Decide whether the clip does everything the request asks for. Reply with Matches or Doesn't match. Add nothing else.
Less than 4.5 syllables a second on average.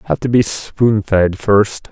Matches